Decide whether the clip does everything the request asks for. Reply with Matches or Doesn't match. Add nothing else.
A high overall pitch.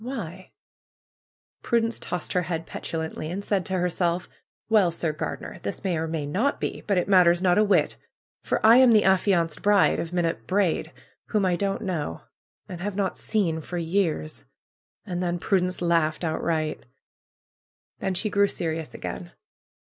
Doesn't match